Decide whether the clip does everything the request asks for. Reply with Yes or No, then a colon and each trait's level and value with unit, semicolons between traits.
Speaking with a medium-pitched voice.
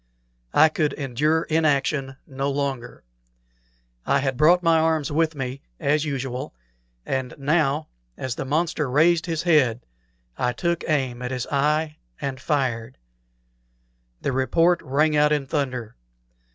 Yes: medium, 145 Hz